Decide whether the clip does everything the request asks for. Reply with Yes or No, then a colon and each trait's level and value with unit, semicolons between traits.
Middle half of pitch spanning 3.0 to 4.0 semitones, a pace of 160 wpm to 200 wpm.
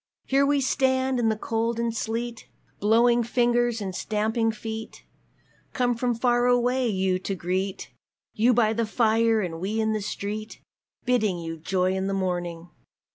Yes: average, 3.7 semitones; average, 165 wpm